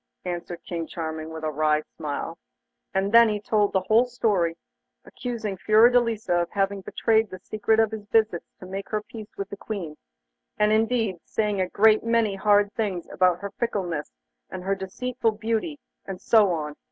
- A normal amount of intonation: Yes, average, 3.6 semitones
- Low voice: No, high, 205 Hz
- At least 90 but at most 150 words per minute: No, average, 175 wpm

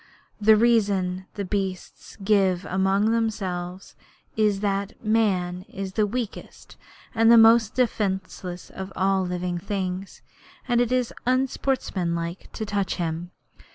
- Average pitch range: Yes, average, 3.1 semitones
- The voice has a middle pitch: No, high, 195 Hz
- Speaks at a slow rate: Yes, slow, 120 wpm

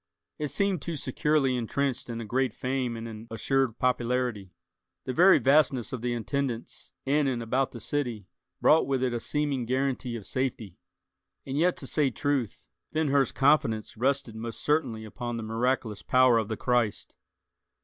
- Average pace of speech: Yes, average, 170 wpm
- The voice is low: Yes, low, 125 Hz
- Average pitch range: Yes, average, 3.2 semitones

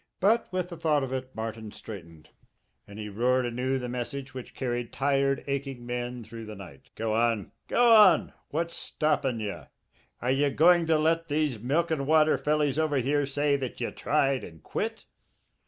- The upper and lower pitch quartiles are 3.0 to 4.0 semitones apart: No, average, 4.4 semitones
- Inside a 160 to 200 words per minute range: Yes, average, 180 wpm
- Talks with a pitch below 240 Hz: Yes, low, 135 Hz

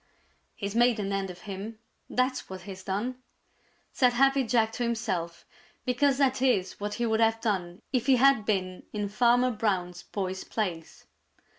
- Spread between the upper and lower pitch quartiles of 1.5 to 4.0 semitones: No, average, 4.4 semitones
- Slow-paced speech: No, average, 165 wpm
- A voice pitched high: Yes, high, 220 Hz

